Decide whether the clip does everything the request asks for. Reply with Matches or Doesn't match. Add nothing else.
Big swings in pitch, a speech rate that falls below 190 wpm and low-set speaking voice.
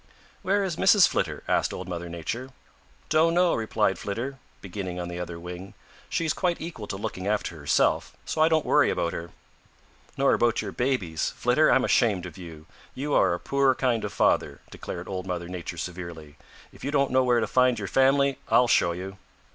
Doesn't match